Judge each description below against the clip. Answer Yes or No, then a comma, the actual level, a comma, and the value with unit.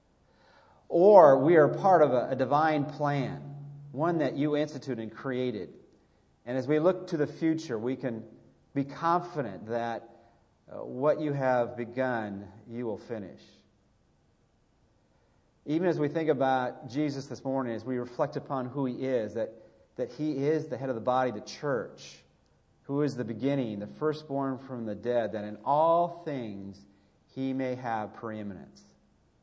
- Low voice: Yes, low, 130 Hz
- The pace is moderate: Yes, average, 155 wpm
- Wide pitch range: No, average, 4.2 semitones